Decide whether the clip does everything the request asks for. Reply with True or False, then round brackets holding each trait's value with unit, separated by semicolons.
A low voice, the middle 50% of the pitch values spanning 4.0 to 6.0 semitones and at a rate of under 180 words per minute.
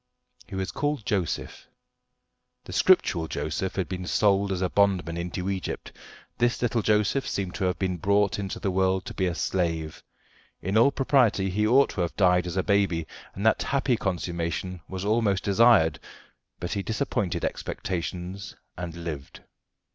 False (95 Hz; 2.8 semitones; 160 wpm)